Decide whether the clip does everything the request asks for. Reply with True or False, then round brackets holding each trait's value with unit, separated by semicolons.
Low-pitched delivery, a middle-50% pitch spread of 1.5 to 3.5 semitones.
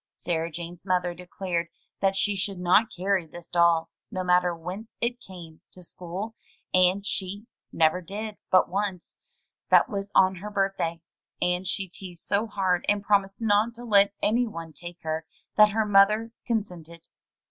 False (190 Hz; 2.9 semitones)